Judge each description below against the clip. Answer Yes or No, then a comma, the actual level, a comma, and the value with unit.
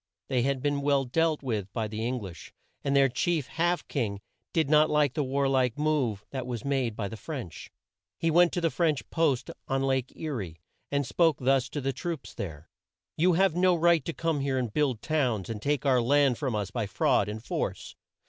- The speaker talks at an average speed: No, fast, 215 wpm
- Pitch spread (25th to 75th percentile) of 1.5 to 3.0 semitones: No, average, 4.6 semitones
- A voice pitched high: No, low, 135 Hz